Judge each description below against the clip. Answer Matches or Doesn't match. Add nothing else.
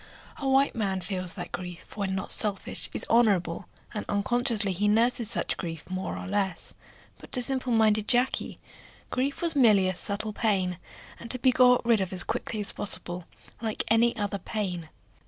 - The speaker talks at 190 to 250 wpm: Doesn't match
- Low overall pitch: Doesn't match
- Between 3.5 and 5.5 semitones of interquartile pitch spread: Matches